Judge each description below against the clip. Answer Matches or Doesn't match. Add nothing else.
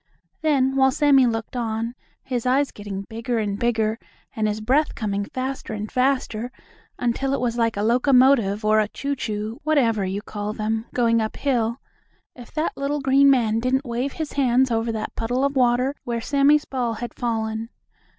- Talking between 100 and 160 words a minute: Doesn't match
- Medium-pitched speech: Doesn't match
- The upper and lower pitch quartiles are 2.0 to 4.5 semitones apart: Matches